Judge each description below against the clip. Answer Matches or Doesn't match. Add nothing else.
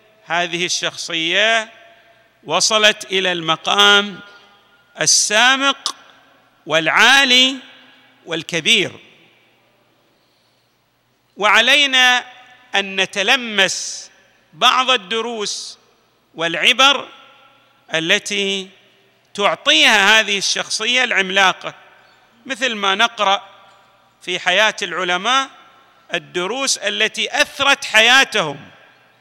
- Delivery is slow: Matches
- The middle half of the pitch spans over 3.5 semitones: Matches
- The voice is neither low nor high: Doesn't match